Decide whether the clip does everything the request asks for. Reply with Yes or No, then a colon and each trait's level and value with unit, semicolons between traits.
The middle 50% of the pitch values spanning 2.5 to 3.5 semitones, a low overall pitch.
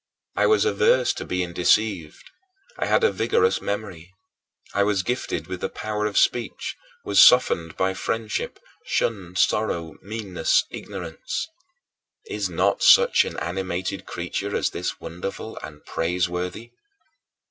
No: average, 3.9 semitones; very low, 95 Hz